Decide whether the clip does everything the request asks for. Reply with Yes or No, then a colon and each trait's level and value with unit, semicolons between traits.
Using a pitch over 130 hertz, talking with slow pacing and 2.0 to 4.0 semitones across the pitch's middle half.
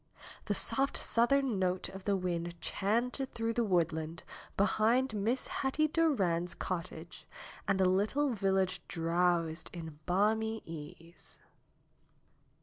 No: high, 190 Hz; slow, 115 wpm; average, 5.0 semitones